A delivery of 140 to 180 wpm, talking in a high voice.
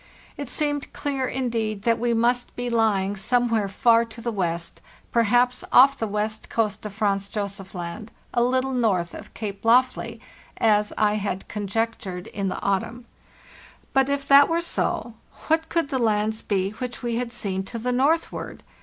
Yes: average, 170 wpm; high, 230 Hz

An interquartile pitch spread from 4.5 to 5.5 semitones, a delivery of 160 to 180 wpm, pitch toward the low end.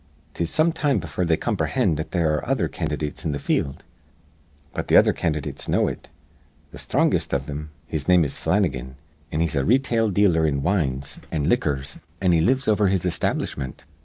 No: average, 4.8 semitones; average, 190 wpm; very low, 80 Hz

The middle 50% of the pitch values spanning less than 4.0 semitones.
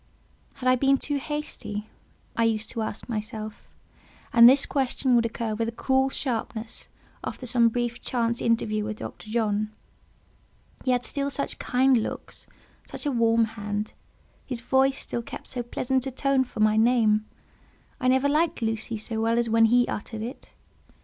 Yes: average, 2.9 semitones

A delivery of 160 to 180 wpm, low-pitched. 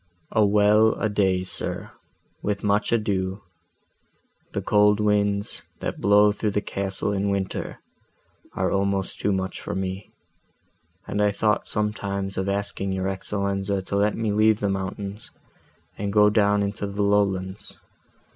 No: average, 145 wpm; low, 100 Hz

